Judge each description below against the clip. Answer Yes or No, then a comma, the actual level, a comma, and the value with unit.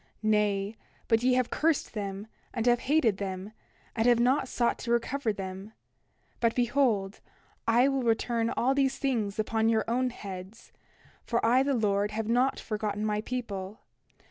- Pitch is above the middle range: Yes, high, 230 Hz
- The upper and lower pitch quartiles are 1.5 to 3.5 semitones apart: Yes, average, 3.2 semitones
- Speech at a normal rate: Yes, average, 160 wpm